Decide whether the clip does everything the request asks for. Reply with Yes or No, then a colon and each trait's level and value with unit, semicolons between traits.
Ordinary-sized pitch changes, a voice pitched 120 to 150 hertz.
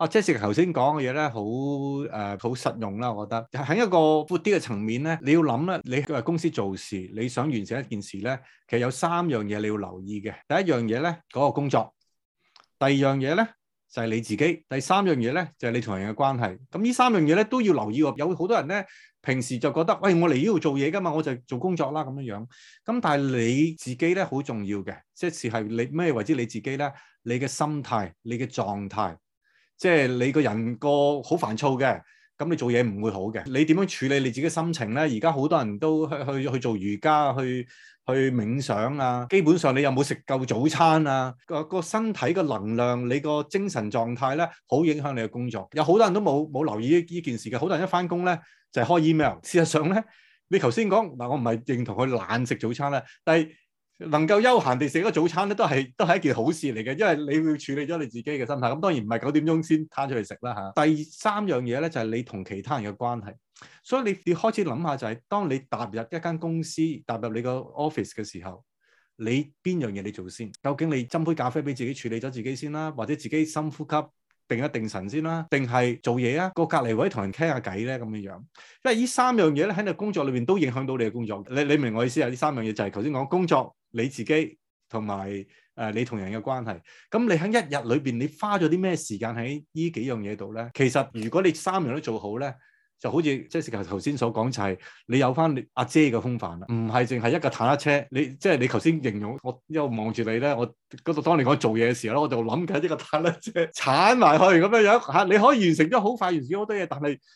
No: wide, 5.7 semitones; medium, 140 Hz